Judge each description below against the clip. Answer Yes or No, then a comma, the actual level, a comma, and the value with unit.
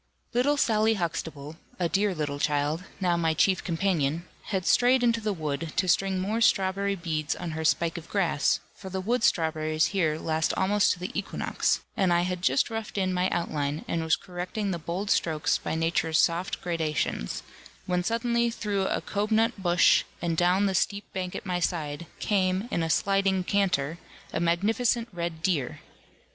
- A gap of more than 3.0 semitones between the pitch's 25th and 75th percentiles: Yes, average, 3.6 semitones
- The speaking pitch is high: No, medium, 180 Hz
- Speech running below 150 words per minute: No, average, 175 wpm